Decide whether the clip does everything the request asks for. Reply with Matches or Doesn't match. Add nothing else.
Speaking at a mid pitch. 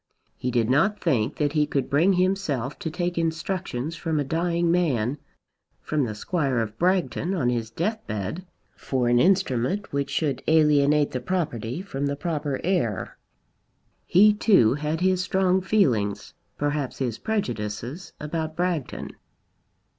Matches